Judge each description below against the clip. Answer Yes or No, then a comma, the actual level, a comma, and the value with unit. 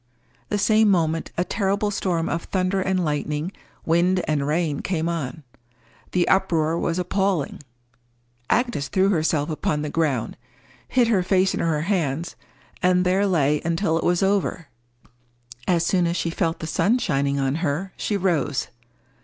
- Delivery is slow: No, average, 155 wpm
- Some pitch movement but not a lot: Yes, average, 3.6 semitones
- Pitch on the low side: No, medium, 170 Hz